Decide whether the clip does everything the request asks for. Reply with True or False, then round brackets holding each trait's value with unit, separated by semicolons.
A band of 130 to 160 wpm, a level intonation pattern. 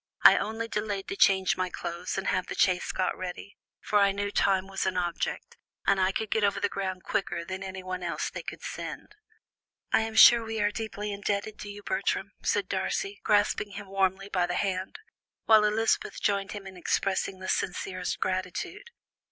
False (190 wpm; 2.0 semitones)